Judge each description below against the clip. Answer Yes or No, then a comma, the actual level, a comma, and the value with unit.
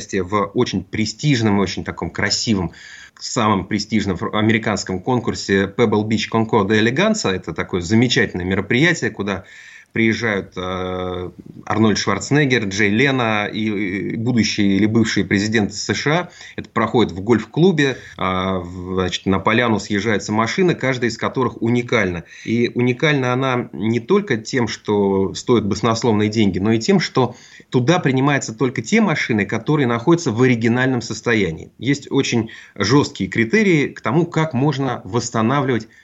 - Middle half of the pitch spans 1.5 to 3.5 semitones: No, average, 3.9 semitones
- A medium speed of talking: Yes, average, 130 wpm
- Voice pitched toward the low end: Yes, low, 110 Hz